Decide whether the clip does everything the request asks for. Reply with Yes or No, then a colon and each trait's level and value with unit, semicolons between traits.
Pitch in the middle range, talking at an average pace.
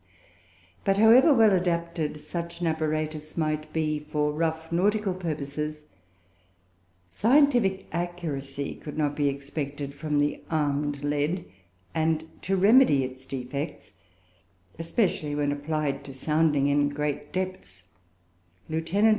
No: medium, 155 Hz; slow, 115 wpm